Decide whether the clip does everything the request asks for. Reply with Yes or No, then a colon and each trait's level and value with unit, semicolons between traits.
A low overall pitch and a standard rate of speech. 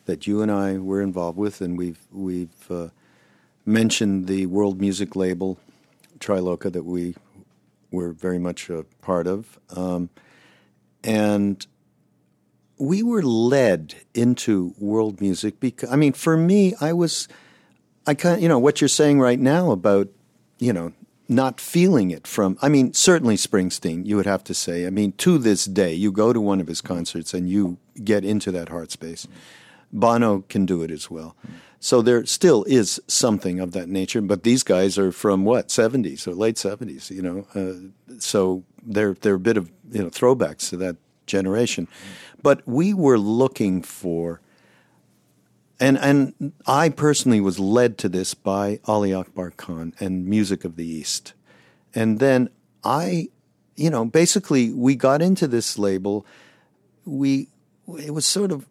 Yes: low, 100 Hz; average, 165 wpm